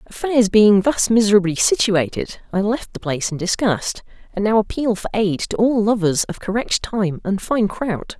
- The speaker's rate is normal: Yes, average, 185 wpm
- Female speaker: Yes, female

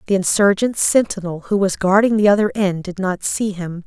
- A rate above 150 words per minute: Yes, average, 200 wpm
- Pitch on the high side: Yes, high, 195 Hz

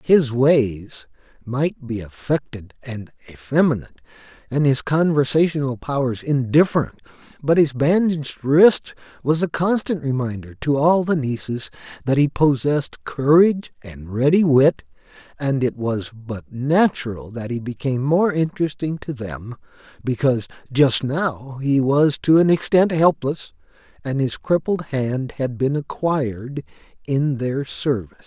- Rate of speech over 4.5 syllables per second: No, 4.4 syllables/s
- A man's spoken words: Yes, male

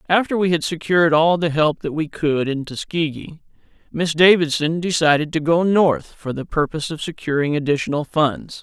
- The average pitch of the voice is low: No, medium, 160 Hz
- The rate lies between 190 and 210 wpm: No, average, 175 wpm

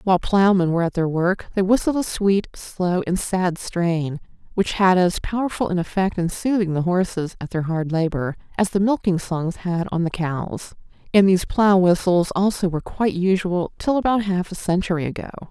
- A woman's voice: Yes, female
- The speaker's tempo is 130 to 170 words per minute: No, average, 195 wpm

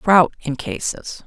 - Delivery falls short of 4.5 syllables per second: Yes, 3.5 syllables/s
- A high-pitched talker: No, medium, 165 Hz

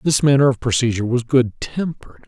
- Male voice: Yes, male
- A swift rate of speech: No, average, 185 wpm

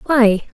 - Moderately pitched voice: No, high, 240 Hz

